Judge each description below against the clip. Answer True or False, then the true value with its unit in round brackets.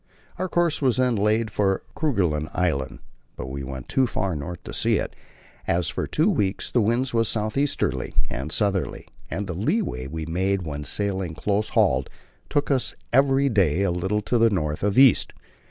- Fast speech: False (185 wpm)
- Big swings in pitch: True (6.9 semitones)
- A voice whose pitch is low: True (100 Hz)